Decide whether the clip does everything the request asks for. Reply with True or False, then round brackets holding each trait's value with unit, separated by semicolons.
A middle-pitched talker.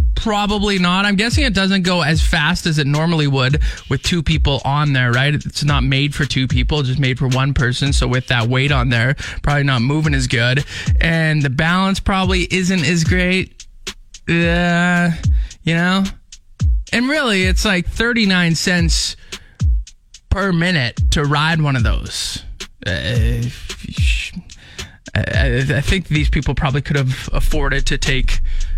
True (145 Hz)